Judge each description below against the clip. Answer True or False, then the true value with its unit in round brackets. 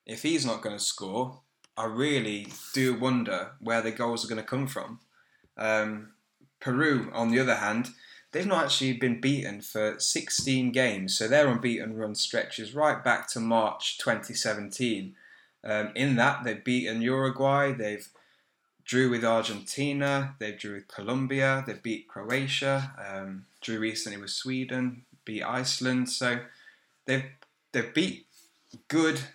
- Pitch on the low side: True (120 Hz)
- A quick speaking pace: False (145 wpm)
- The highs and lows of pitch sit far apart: False (3.6 semitones)